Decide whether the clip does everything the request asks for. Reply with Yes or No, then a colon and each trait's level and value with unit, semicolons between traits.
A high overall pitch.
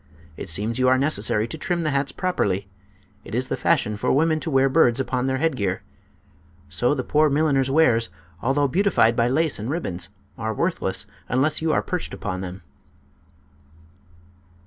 No: low, 130 Hz